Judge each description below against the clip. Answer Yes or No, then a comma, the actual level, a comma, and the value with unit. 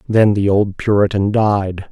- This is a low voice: Yes, low, 100 Hz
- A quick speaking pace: No, average, 155 wpm